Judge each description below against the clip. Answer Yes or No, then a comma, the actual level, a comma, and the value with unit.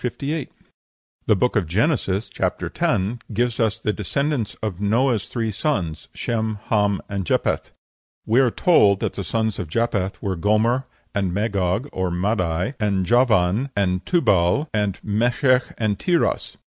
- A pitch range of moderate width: Yes, average, 4.0 semitones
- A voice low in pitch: Yes, low, 105 Hz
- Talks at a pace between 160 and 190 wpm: No, average, 145 wpm